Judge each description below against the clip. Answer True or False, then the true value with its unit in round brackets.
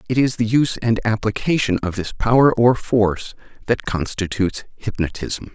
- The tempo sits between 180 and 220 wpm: False (150 wpm)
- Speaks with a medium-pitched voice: False (110 Hz)